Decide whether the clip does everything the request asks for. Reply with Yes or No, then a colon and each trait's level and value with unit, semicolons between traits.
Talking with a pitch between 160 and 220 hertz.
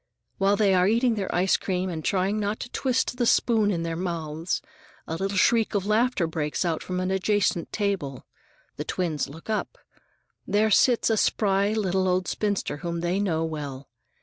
Yes: high, 190 Hz